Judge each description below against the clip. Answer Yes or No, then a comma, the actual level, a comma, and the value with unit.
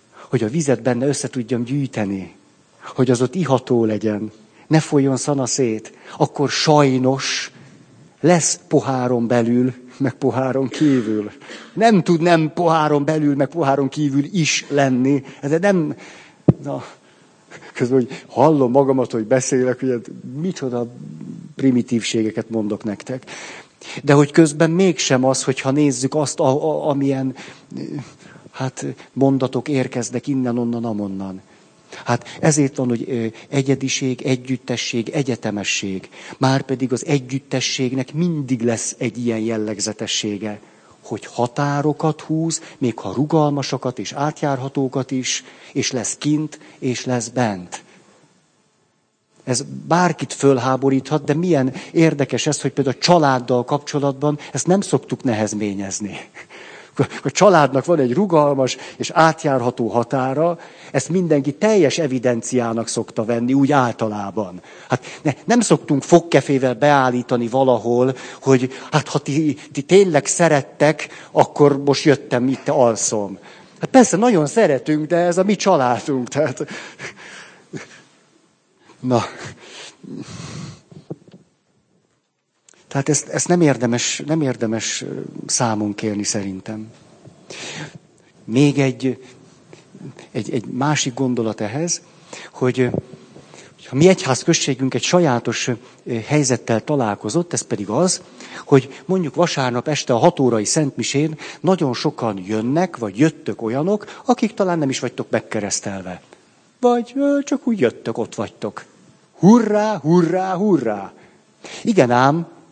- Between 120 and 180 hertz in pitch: Yes, low, 135 Hz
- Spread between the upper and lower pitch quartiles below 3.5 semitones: No, average, 4.0 semitones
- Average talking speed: Yes, average, 115 wpm